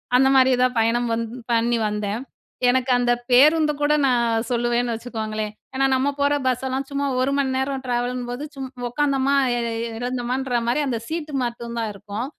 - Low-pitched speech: No, high, 245 Hz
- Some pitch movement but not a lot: No, narrow, 2.1 semitones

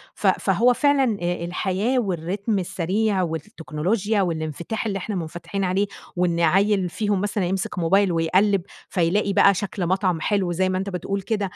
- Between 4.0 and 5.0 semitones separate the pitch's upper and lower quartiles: No, average, 2.8 semitones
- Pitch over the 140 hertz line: Yes, high, 190 Hz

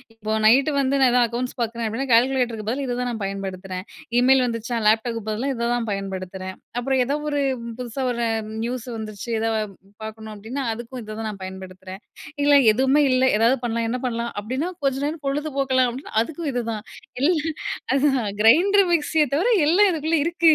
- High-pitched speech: Yes, high, 245 Hz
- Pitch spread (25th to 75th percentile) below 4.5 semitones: Yes, average, 4.0 semitones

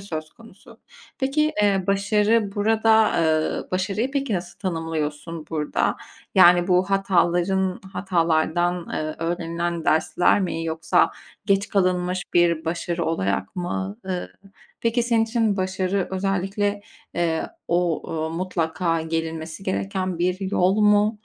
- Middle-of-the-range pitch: Yes, medium, 180 Hz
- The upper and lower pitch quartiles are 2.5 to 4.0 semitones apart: Yes, average, 3.3 semitones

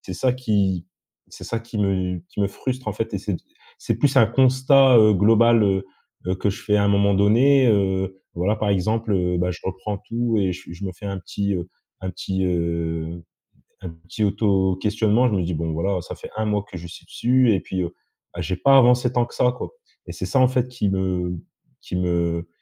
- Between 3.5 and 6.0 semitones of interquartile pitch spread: Yes, average, 4.0 semitones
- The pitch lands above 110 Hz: No, low, 100 Hz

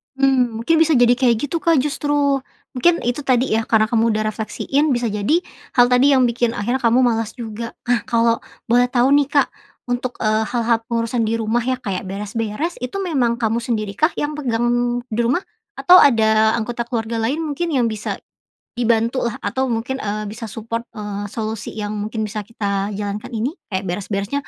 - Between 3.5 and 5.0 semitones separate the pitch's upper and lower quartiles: No, average, 2.9 semitones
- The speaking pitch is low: No, high, 235 Hz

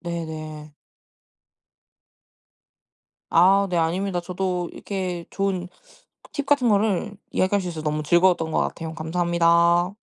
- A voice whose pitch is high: No, medium, 175 Hz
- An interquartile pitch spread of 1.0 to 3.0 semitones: Yes, narrow, 2.6 semitones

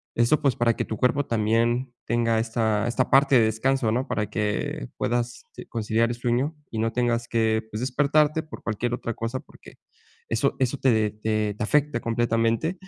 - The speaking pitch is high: No, low, 115 Hz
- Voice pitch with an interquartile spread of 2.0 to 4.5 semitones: Yes, narrow, 2.6 semitones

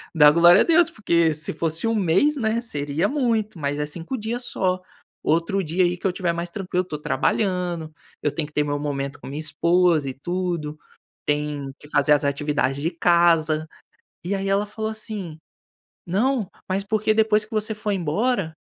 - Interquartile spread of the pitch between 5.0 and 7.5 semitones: Yes, wide, 5.6 semitones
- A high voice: No, medium, 175 Hz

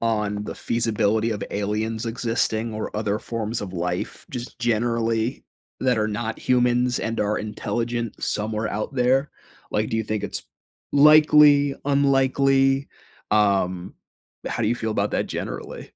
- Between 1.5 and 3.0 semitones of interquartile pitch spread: Yes, average, 2.7 semitones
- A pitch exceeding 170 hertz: No, low, 115 Hz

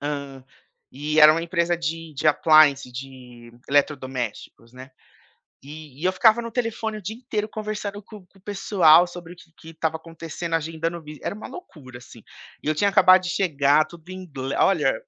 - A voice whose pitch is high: No, medium, 165 Hz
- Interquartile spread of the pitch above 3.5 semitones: Yes, average, 4.7 semitones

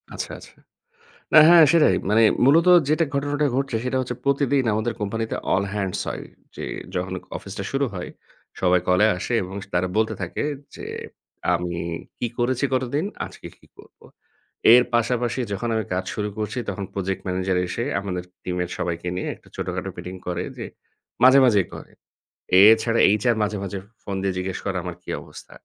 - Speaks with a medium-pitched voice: No, low, 105 Hz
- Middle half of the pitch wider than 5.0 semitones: Yes, wide, 5.4 semitones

